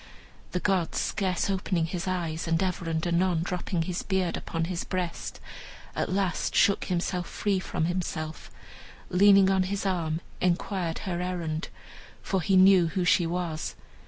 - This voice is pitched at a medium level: Yes, medium, 180 Hz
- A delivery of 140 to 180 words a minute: Yes, average, 160 wpm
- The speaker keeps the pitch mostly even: Yes, narrow, 2.2 semitones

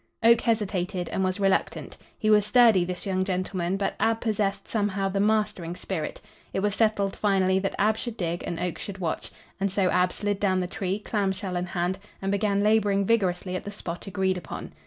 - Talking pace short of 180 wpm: No, average, 200 wpm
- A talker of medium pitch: No, high, 195 Hz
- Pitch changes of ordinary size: No, narrow, 2.2 semitones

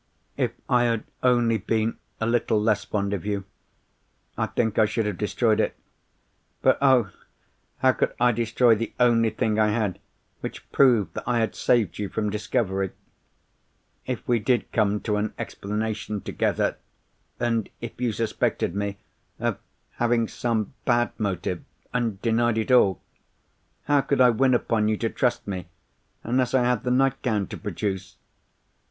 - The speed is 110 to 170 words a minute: Yes, average, 160 wpm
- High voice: No, low, 115 Hz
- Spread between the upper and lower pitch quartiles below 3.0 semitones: Yes, narrow, 2.6 semitones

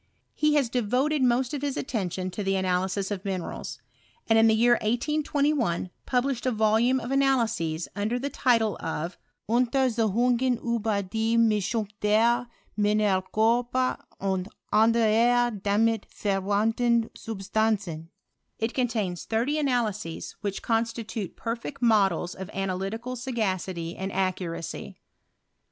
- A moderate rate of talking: No, slow, 120 wpm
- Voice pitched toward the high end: Yes, high, 225 Hz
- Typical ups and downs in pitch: Yes, average, 3.9 semitones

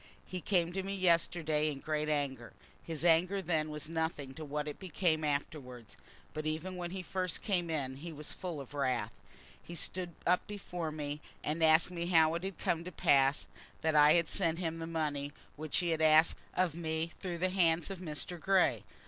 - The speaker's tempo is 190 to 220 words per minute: Yes, average, 200 wpm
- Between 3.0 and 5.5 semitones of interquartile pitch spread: No, narrow, 2.6 semitones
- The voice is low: No, medium, 160 Hz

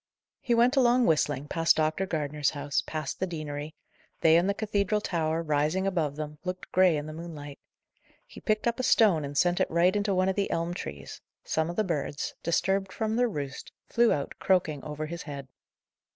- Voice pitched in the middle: Yes, medium, 165 Hz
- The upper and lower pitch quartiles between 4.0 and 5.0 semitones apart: Yes, average, 4.5 semitones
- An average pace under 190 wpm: No, average, 195 wpm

